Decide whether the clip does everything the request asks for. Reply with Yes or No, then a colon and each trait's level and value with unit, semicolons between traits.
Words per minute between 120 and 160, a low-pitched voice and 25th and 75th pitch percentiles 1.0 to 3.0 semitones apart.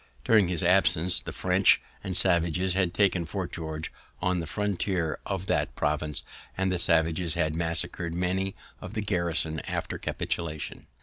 Yes: average, 150 wpm; very low, 85 Hz; narrow, 2.5 semitones